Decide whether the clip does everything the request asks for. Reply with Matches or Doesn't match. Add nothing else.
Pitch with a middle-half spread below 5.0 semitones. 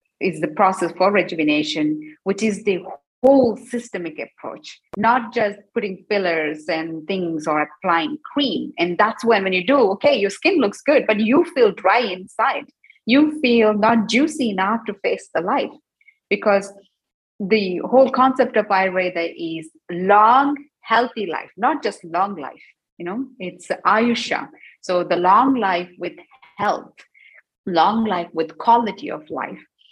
Doesn't match